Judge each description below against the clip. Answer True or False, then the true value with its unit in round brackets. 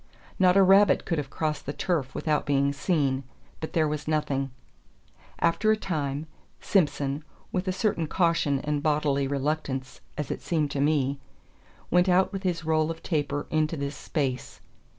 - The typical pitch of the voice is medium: True (150 Hz)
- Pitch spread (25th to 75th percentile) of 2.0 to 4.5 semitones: True (3.1 semitones)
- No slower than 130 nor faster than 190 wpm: True (165 wpm)